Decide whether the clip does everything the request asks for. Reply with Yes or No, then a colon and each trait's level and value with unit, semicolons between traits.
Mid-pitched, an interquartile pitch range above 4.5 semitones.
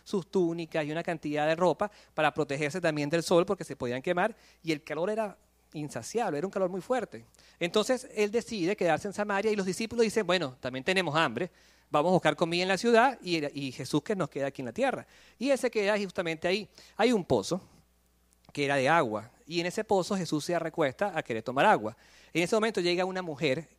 Yes: medium, 175 Hz; average, 5.1 semitones